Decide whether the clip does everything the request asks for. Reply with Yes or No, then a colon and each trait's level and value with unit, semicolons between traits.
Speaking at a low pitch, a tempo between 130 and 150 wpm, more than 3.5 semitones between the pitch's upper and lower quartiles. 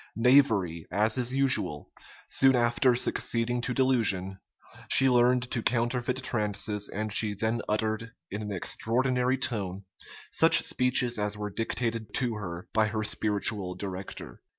No: low, 115 Hz; slow, 135 wpm; average, 3.1 semitones